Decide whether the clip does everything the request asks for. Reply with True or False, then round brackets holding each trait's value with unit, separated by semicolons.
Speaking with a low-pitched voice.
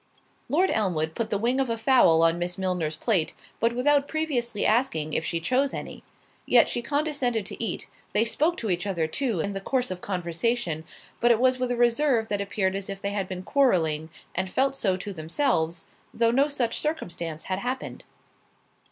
False (215 Hz)